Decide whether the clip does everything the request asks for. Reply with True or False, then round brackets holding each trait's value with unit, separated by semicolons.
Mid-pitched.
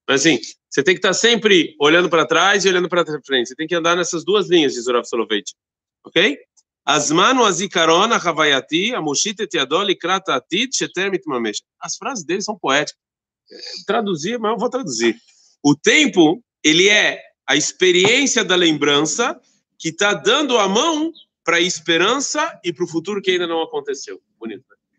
False (205 Hz)